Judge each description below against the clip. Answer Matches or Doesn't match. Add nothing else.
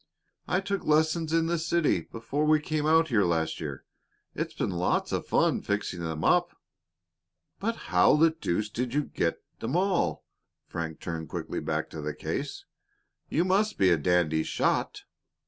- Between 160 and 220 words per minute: Matches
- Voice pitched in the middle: Doesn't match